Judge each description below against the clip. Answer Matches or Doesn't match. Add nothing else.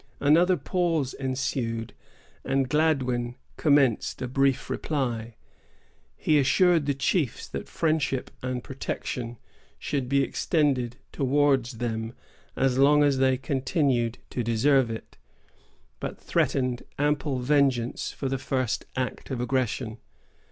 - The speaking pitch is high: Doesn't match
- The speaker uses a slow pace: Matches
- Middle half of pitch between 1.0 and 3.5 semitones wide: Matches